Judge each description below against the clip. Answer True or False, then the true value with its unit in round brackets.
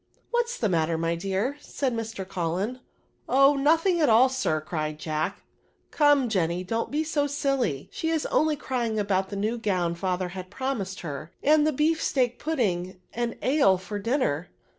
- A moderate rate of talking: True (185 wpm)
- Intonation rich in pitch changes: True (7.6 semitones)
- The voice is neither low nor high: False (225 Hz)